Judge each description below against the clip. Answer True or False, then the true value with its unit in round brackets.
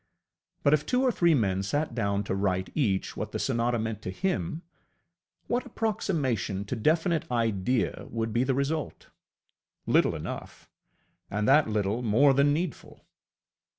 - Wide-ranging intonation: True (6.7 semitones)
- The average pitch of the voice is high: False (125 Hz)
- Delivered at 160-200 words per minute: False (150 wpm)